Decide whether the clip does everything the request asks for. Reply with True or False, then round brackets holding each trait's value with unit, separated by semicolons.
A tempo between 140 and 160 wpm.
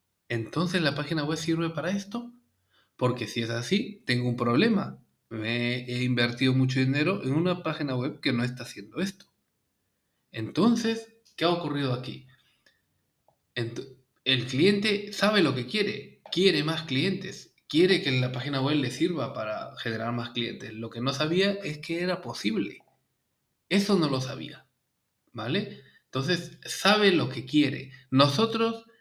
True (150 wpm)